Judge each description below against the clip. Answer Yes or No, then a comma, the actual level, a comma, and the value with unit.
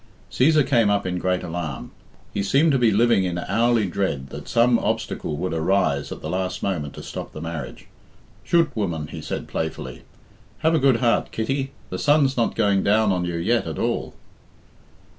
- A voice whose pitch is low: Yes, low, 100 Hz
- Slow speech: No, average, 190 wpm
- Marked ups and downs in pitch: Yes, wide, 5.9 semitones